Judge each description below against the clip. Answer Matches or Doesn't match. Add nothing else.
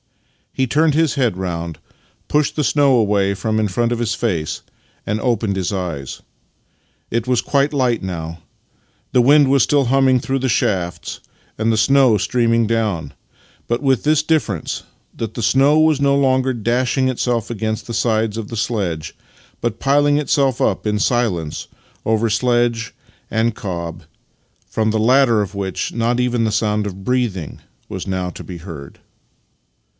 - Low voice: Matches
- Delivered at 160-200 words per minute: Matches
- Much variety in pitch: Doesn't match